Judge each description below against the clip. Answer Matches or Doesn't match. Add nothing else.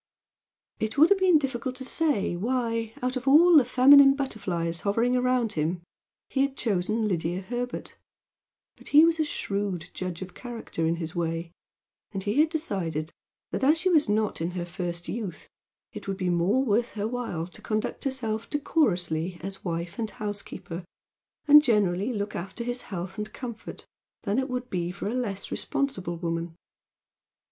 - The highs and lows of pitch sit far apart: Matches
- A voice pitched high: Matches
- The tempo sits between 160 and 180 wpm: Matches